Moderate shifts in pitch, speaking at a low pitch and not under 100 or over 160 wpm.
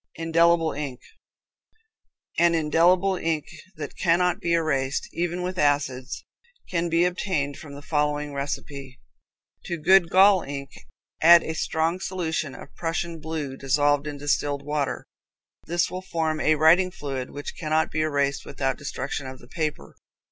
No: average, 3.0 semitones; medium, 155 Hz; average, 145 wpm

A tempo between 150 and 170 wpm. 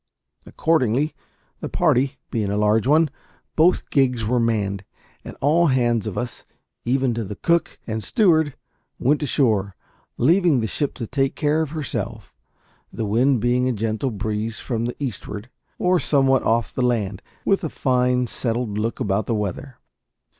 Yes: average, 160 wpm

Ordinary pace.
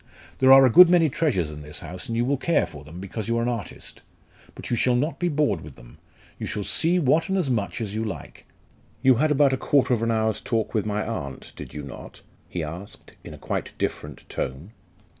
No: fast, 235 wpm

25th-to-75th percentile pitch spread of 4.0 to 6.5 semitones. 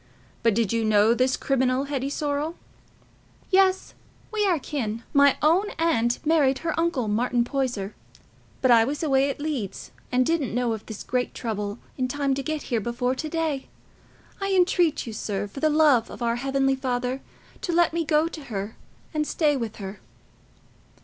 Yes: average, 4.7 semitones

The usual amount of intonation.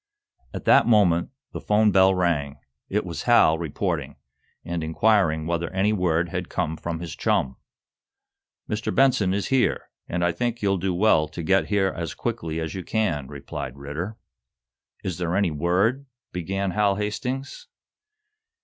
Yes: average, 4.1 semitones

